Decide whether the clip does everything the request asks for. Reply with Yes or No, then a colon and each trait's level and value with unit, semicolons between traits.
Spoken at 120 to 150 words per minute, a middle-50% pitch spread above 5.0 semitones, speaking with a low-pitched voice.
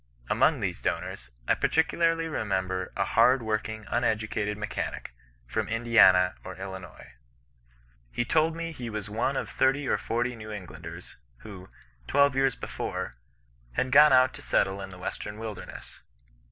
Yes: average, 145 wpm; wide, 5.5 semitones; low, 110 Hz